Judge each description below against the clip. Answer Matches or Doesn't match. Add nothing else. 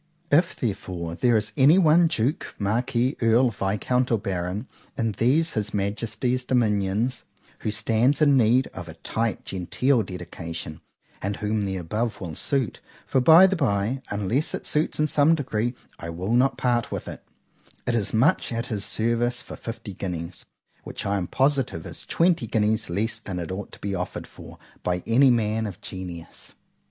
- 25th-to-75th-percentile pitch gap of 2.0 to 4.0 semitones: Doesn't match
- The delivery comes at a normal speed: Matches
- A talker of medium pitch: Doesn't match